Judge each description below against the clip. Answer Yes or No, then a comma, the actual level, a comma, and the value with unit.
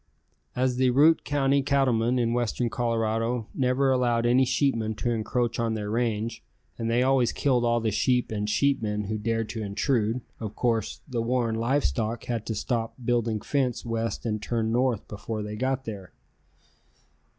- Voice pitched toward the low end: Yes, low, 115 Hz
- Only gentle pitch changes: Yes, narrow, 2.2 semitones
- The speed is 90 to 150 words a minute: No, average, 170 wpm